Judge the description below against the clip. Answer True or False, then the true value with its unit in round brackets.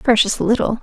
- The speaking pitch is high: True (220 Hz)